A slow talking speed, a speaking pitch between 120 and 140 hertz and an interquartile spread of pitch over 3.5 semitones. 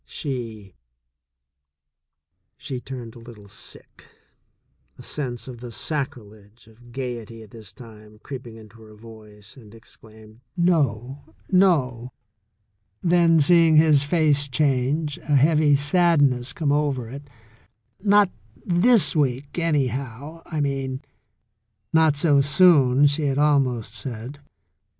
Yes: slow, 115 wpm; low, 135 Hz; average, 4.6 semitones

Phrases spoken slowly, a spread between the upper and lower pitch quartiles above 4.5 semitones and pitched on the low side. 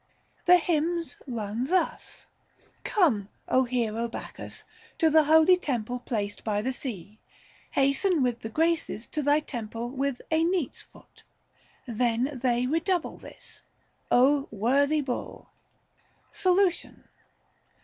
No: slow, 130 wpm; average, 5.3 semitones; very high, 265 Hz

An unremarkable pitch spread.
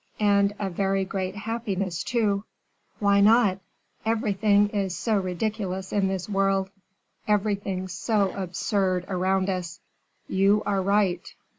No: narrow, 1.6 semitones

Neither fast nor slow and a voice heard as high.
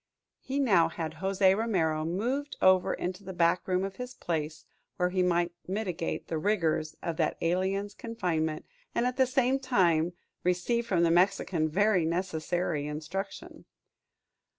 No: average, 150 wpm; medium, 180 Hz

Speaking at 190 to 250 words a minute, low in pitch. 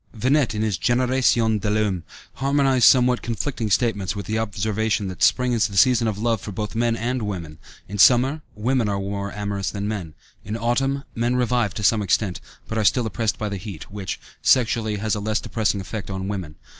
Yes: average, 200 wpm; low, 110 Hz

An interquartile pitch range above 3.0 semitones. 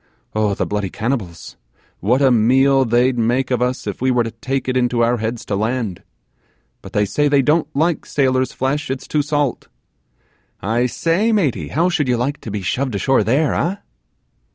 Yes: average, 3.7 semitones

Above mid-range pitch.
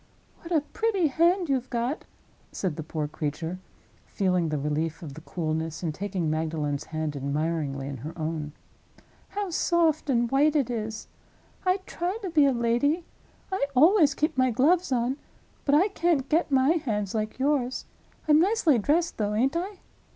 Yes: high, 245 Hz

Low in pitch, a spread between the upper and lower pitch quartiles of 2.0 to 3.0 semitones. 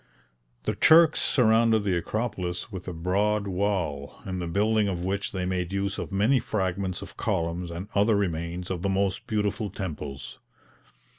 Yes: very low, 95 Hz; average, 2.7 semitones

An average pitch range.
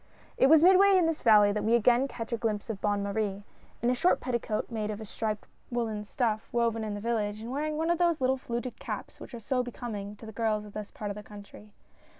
Yes: average, 3.1 semitones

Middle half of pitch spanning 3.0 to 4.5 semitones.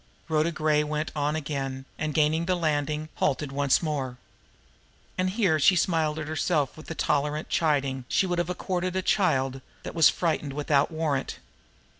No: narrow, 2.5 semitones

